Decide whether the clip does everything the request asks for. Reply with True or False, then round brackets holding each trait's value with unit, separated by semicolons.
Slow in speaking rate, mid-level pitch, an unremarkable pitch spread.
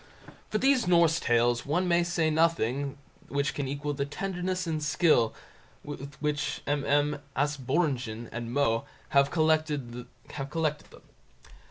True (125 wpm; 145 Hz; 3.2 semitones)